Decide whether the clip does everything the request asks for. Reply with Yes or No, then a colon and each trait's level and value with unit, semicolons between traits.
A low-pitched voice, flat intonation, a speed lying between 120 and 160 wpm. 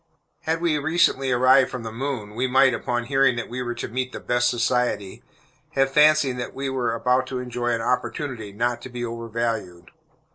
No: low, 125 Hz; narrow, 2.1 semitones; average, 190 wpm